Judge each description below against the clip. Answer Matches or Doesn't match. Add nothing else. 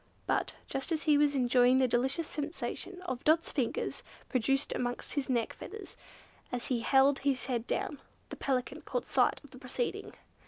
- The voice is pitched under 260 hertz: Doesn't match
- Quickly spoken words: Doesn't match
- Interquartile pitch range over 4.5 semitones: Doesn't match